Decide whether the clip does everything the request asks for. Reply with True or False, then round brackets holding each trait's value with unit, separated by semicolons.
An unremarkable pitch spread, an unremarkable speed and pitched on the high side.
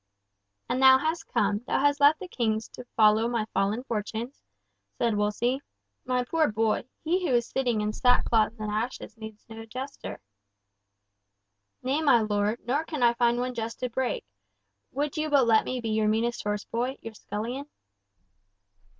True (3.3 semitones; 165 wpm; 235 Hz)